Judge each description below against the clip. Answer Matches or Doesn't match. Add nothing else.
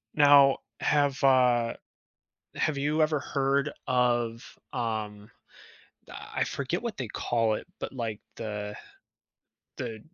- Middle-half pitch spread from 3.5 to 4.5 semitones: Matches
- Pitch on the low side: Matches